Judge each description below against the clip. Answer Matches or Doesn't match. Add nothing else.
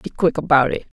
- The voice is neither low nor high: Matches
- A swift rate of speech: Matches